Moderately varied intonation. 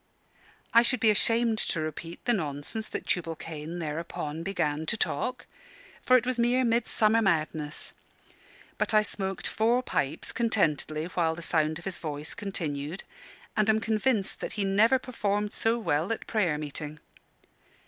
No: wide, 6.4 semitones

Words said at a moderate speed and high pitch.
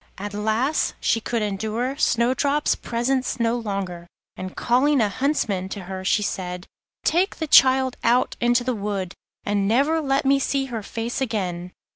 Yes: average, 160 wpm; high, 230 Hz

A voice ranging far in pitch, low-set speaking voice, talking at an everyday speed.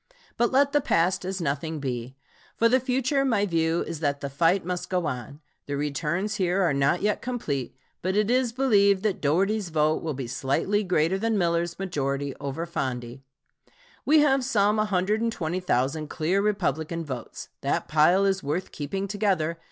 No: wide, 5.8 semitones; medium, 175 Hz; average, 165 wpm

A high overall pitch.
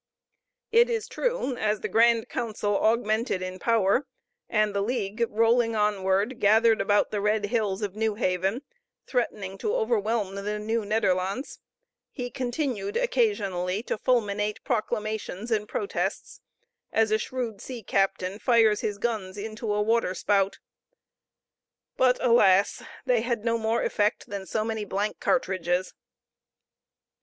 Yes: high, 215 Hz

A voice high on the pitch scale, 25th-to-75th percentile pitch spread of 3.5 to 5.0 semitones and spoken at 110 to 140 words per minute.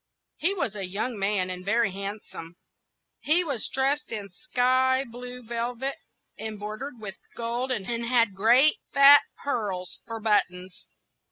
Yes: high, 230 Hz; average, 4.4 semitones; slow, 135 wpm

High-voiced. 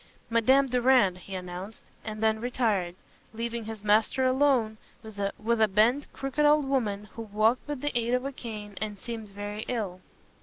Yes: high, 220 Hz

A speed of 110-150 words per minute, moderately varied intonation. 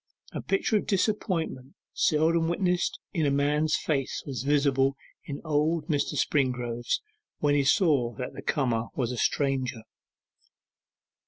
Yes: slow, 135 wpm; average, 3.5 semitones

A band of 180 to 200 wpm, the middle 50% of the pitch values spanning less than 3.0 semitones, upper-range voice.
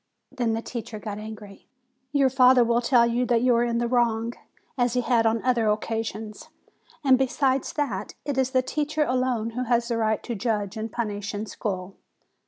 Yes: average, 190 wpm; narrow, 2.5 semitones; high, 235 Hz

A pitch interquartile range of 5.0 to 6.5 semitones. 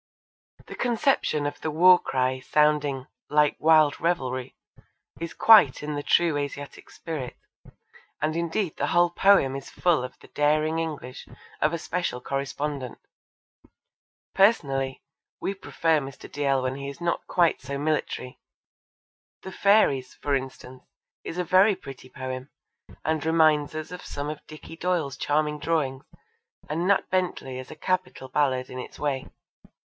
No: average, 3.8 semitones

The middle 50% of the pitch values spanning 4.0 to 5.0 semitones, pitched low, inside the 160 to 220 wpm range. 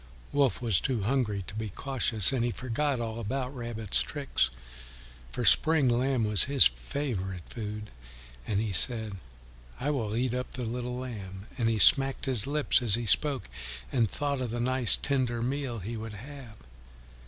No: average, 3.6 semitones; low, 120 Hz; average, 170 wpm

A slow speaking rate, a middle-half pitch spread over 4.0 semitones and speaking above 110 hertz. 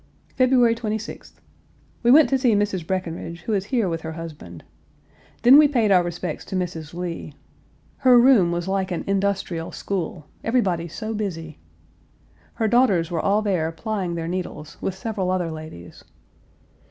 No: average, 155 wpm; average, 4.7 semitones; medium, 185 Hz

